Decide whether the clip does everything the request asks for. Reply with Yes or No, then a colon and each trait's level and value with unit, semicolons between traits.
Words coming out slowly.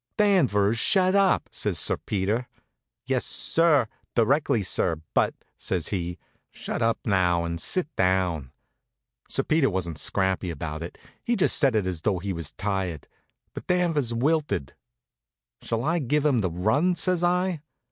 No: average, 155 wpm